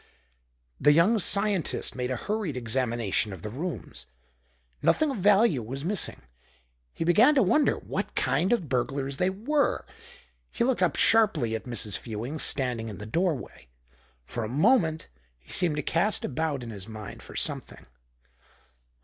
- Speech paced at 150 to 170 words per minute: Yes, average, 155 wpm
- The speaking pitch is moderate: Yes, medium, 150 Hz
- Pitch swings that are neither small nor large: No, wide, 9.0 semitones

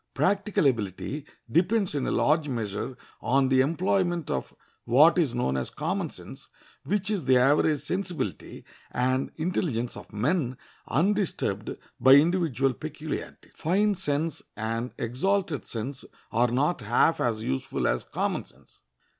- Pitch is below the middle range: No, medium, 145 Hz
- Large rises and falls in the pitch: Yes, wide, 6.0 semitones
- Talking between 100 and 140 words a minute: Yes, slow, 135 wpm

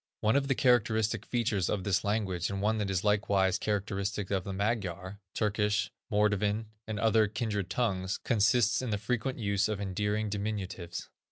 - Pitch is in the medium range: No, low, 105 Hz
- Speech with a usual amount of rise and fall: No, narrow, 2.0 semitones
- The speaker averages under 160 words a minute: No, average, 165 wpm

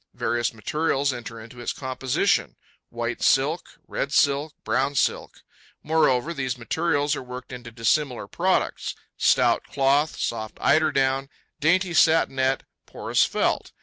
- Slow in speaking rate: Yes, slow, 120 wpm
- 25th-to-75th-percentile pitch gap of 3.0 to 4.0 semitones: Yes, average, 3.5 semitones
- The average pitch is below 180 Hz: Yes, low, 135 Hz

